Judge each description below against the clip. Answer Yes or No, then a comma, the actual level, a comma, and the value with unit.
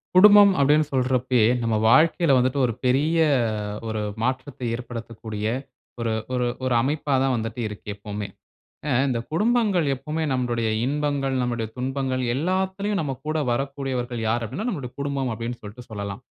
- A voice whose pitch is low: Yes, low, 130 Hz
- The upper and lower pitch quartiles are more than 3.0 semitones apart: Yes, average, 4.0 semitones